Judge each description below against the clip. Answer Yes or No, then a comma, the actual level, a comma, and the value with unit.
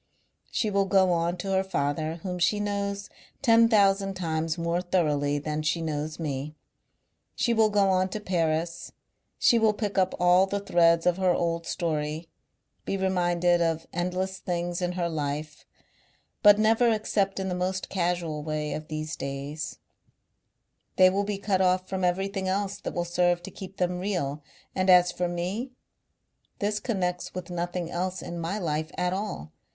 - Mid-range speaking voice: Yes, medium, 180 Hz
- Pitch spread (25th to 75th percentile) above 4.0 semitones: No, average, 2.7 semitones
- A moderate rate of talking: Yes, average, 170 wpm